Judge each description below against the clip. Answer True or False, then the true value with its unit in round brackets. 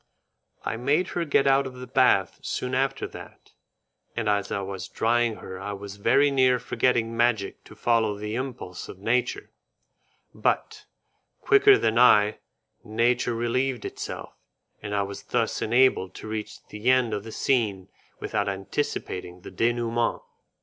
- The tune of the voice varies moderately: True (3.7 semitones)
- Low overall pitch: True (115 Hz)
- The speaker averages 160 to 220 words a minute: False (150 wpm)